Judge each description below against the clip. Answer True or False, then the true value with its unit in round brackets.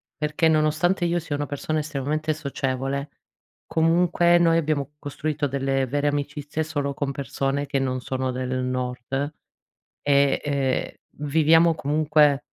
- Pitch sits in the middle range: True (145 Hz)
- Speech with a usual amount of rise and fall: False (2.3 semitones)